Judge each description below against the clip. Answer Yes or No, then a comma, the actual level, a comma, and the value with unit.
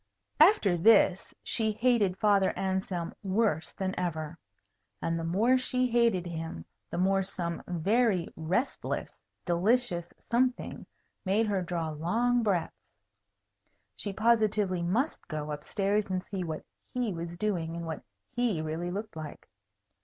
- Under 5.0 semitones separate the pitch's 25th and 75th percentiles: Yes, average, 4.5 semitones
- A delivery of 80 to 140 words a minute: Yes, slow, 135 wpm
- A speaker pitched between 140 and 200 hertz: Yes, high, 190 Hz